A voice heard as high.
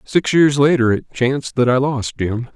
No: low, 130 Hz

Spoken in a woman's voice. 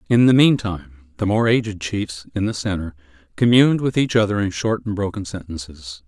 No: male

